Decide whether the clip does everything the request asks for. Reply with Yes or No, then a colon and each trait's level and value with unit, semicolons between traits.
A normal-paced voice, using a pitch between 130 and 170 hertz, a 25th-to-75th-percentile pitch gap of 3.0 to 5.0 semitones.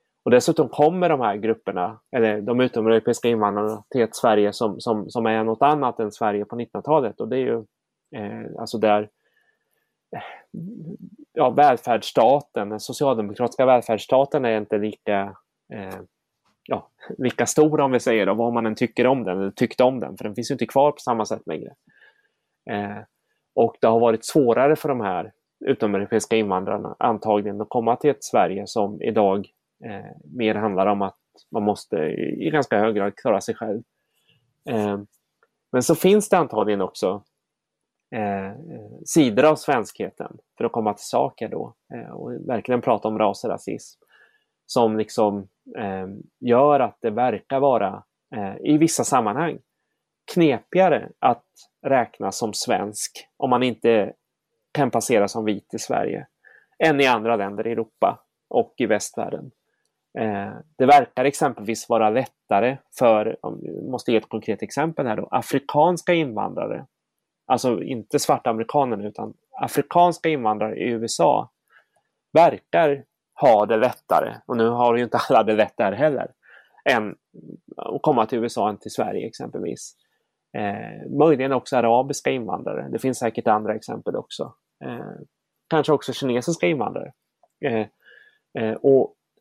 No: average, 150 wpm; low, 115 Hz; average, 4.5 semitones